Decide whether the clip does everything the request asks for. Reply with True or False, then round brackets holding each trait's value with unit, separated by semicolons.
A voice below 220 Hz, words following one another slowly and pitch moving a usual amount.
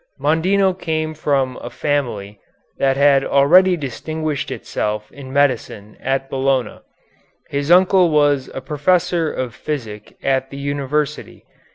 True (140 Hz; 125 wpm; 3.0 semitones)